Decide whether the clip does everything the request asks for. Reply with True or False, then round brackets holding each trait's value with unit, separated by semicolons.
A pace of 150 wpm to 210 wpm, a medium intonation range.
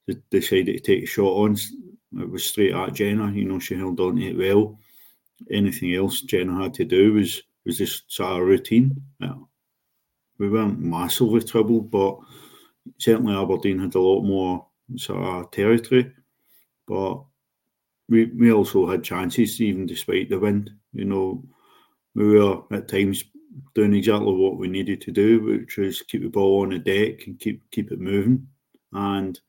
True (170 wpm; 3.7 semitones)